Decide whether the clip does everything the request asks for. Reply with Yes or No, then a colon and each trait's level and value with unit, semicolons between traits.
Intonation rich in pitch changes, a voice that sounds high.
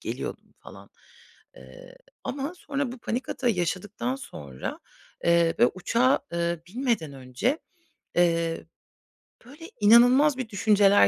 Yes: wide, 7.3 semitones; high, 225 Hz